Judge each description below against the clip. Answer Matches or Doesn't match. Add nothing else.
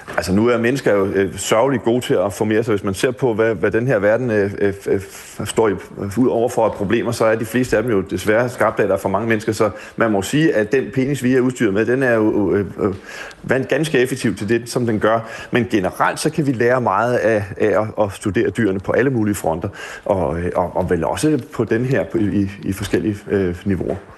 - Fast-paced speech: Matches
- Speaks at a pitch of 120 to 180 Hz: Doesn't match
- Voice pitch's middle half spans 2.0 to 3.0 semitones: Doesn't match